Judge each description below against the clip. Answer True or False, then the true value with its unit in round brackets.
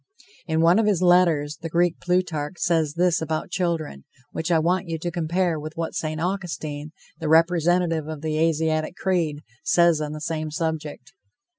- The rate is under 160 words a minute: False (170 wpm)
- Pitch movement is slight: True (2.1 semitones)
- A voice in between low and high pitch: True (165 Hz)